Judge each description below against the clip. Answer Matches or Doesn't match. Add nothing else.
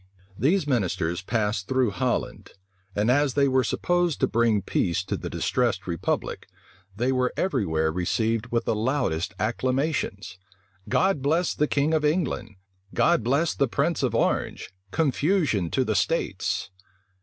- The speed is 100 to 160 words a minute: Matches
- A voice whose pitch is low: Matches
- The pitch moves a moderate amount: Doesn't match